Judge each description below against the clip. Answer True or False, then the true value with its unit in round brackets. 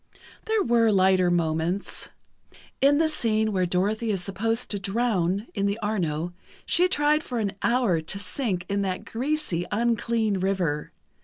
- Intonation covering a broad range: False (4.3 semitones)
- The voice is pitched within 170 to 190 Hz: False (205 Hz)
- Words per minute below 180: True (150 wpm)